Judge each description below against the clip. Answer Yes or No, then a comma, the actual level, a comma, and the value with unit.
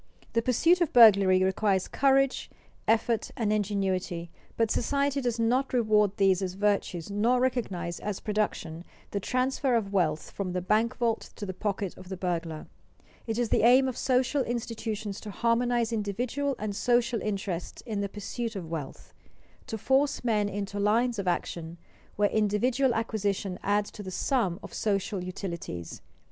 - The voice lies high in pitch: Yes, high, 210 Hz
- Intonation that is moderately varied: Yes, average, 3.9 semitones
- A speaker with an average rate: Yes, average, 160 wpm